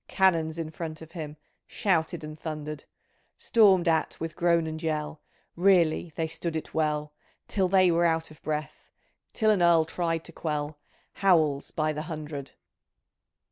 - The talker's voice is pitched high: No, medium, 160 Hz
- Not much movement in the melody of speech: Yes, narrow, 1.9 semitones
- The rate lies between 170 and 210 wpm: No, average, 155 wpm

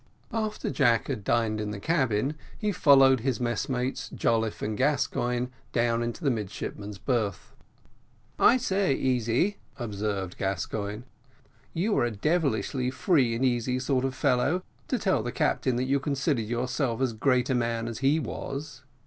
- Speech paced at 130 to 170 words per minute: Yes, average, 155 wpm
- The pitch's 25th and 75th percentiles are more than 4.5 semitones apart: No, average, 3.3 semitones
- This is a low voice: Yes, low, 125 Hz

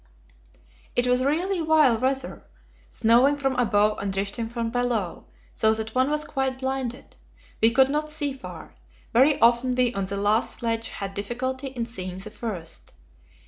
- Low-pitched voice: No, high, 245 Hz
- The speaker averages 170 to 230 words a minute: No, average, 160 wpm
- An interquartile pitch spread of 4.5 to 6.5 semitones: No, average, 3.4 semitones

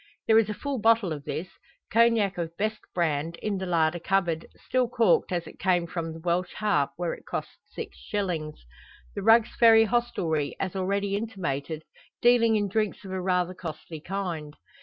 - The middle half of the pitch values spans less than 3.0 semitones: No, average, 4.4 semitones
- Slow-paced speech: No, average, 180 wpm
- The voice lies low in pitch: No, medium, 185 Hz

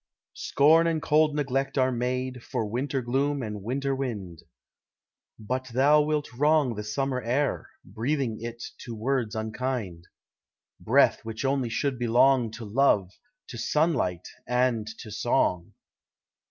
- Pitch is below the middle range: Yes, low, 125 Hz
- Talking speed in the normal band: No, slow, 130 wpm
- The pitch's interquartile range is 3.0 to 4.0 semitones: Yes, average, 3.6 semitones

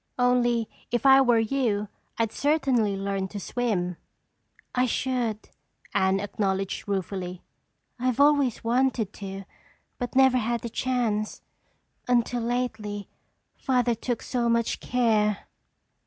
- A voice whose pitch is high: Yes, high, 235 Hz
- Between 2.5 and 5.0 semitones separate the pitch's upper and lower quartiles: Yes, average, 3.4 semitones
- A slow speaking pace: Yes, slow, 115 wpm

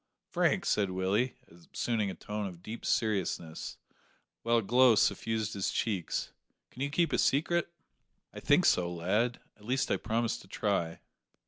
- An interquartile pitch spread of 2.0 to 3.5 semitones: No, average, 4.0 semitones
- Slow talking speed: No, average, 155 wpm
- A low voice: Yes, low, 110 Hz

